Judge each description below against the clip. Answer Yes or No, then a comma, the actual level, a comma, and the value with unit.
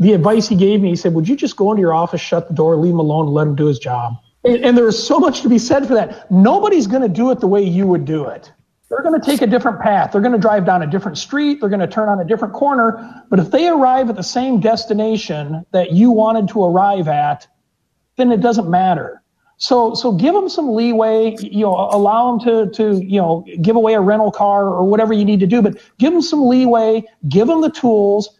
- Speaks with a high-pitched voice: Yes, high, 215 Hz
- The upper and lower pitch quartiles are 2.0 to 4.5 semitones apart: Yes, average, 4.1 semitones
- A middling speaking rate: No, fast, 260 wpm